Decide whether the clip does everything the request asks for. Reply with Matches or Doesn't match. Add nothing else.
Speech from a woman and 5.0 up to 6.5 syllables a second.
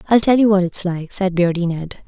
Matches